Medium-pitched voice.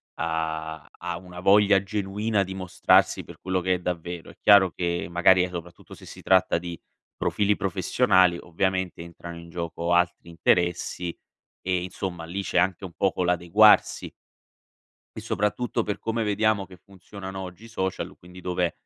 No: very low, 90 Hz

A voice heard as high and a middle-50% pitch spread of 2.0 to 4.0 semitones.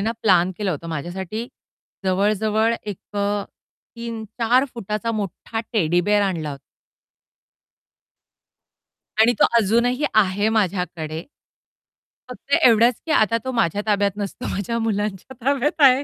Yes: high, 210 Hz; average, 3.5 semitones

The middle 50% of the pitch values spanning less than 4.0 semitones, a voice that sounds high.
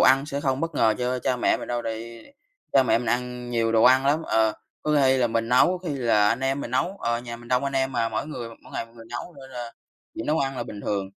No: narrow, 2.6 semitones; low, 125 Hz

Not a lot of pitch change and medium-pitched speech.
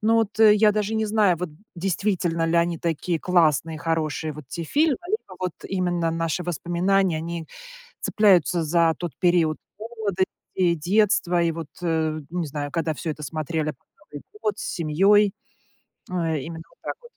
No: average, 3.3 semitones; medium, 170 Hz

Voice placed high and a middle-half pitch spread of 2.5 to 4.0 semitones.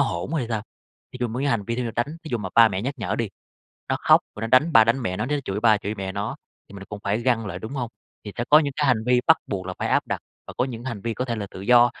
No: low, 115 Hz; average, 3.3 semitones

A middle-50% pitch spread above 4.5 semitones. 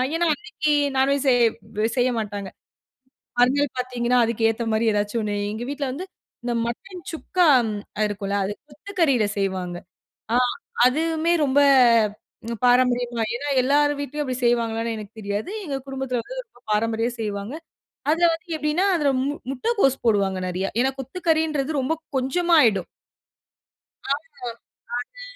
Yes: average, 5.0 semitones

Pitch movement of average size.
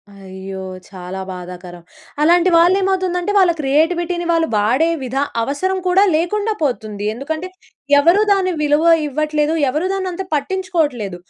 No: wide, 7.7 semitones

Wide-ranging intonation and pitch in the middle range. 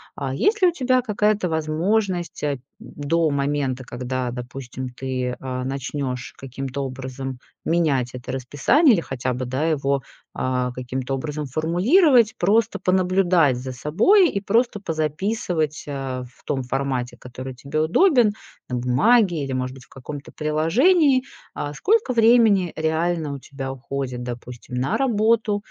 Yes: wide, 7.4 semitones; medium, 145 Hz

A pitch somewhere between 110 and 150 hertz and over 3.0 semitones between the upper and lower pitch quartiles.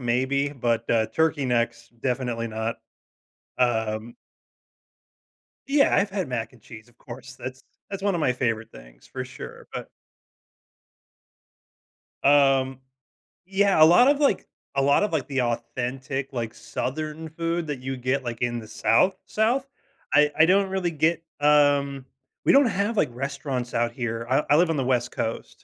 Yes: low, 135 Hz; average, 5.1 semitones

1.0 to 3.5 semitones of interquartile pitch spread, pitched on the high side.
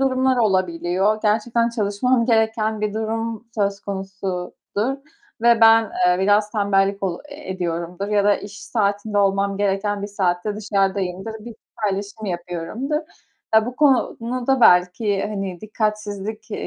Yes: narrow, 2.5 semitones; high, 205 Hz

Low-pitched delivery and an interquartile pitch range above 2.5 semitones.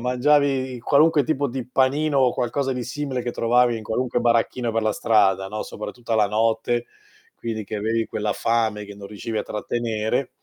Yes: low, 120 Hz; average, 2.9 semitones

